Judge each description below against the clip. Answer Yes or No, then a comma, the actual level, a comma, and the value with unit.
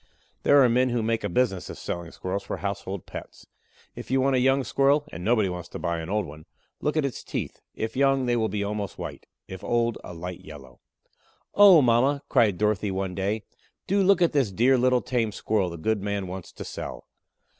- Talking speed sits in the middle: No, fast, 215 wpm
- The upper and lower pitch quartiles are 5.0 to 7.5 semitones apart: Yes, average, 5.3 semitones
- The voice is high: No, low, 110 Hz